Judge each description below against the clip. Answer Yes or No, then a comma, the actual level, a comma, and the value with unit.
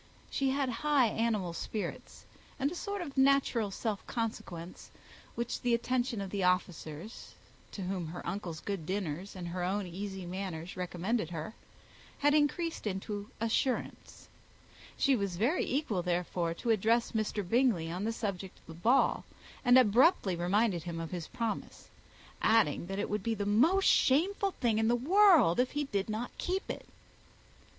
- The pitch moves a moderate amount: No, wide, 5.7 semitones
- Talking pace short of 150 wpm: No, average, 160 wpm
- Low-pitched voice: No, high, 210 Hz